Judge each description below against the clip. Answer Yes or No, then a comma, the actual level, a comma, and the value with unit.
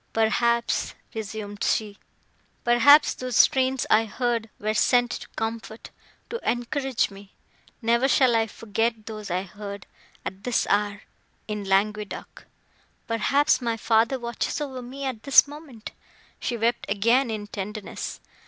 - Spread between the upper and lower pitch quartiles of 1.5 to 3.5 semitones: Yes, average, 2.8 semitones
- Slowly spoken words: Yes, slow, 130 wpm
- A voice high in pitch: Yes, high, 225 Hz